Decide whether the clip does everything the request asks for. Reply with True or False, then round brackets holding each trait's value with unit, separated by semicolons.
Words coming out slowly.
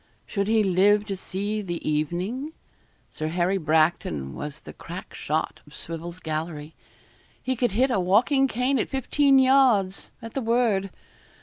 False (150 wpm)